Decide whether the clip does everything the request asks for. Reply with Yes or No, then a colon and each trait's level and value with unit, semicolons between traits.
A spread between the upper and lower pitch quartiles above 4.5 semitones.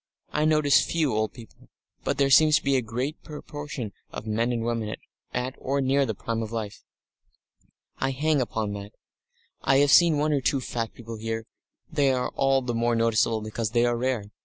No: average, 3.7 semitones